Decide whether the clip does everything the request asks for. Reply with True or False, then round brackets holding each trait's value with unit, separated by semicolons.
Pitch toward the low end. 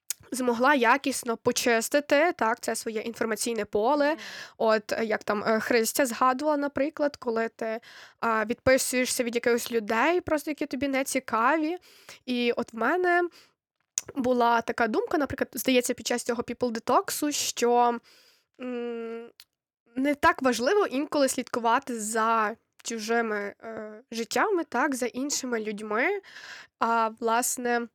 False (245 Hz)